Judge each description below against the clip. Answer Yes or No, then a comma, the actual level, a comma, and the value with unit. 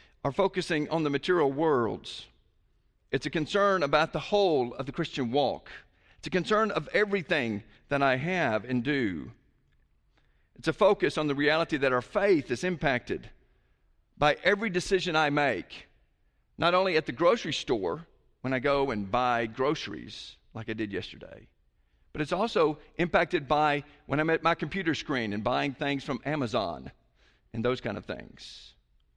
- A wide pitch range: Yes, wide, 5.9 semitones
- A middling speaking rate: Yes, average, 165 wpm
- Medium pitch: Yes, medium, 145 Hz